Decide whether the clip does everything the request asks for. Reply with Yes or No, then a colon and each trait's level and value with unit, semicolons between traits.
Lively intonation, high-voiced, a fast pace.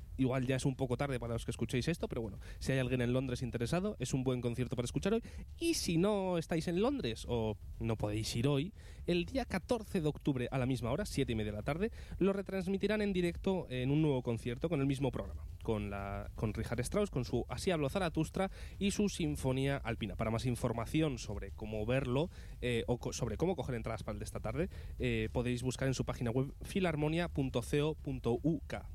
No: wide, 5.7 semitones; low, 130 Hz; fast, 220 wpm